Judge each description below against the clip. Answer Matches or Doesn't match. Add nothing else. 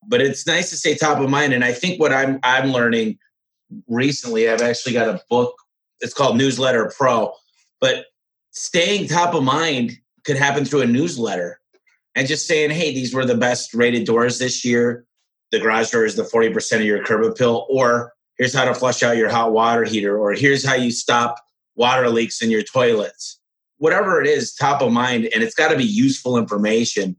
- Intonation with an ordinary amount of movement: Matches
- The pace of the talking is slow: Doesn't match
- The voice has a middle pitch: Doesn't match